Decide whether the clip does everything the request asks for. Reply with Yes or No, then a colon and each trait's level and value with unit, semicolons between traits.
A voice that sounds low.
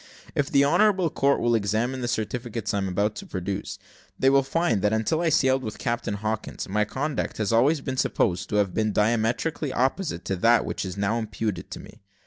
Yes: low, 115 Hz